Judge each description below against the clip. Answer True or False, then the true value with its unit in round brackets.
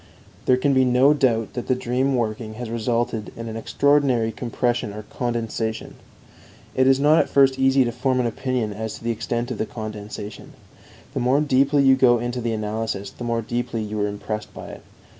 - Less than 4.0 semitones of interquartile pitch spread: True (2.9 semitones)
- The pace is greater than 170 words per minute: True (195 wpm)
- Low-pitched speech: True (120 Hz)